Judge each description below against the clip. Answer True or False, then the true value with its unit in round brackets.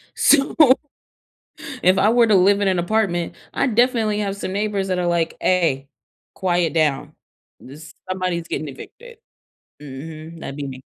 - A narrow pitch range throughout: False (4.3 semitones)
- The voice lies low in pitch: False (180 Hz)